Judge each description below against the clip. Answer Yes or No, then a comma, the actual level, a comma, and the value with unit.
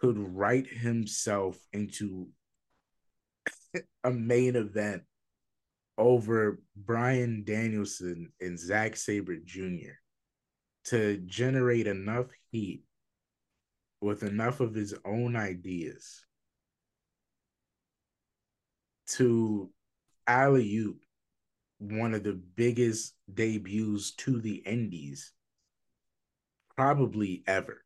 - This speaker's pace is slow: Yes, slow, 80 wpm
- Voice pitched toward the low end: Yes, low, 105 Hz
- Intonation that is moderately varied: Yes, average, 3.1 semitones